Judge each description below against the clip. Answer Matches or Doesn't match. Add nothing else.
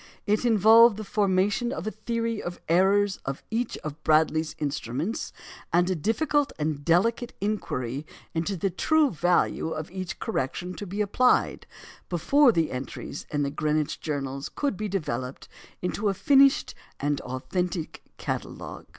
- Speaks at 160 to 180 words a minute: Doesn't match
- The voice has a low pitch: Doesn't match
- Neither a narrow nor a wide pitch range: Doesn't match